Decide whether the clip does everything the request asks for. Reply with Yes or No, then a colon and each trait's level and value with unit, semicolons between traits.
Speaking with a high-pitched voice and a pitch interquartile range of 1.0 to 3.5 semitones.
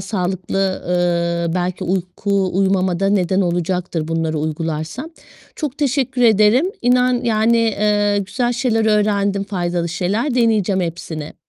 No: high, 195 Hz; average, 4.1 semitones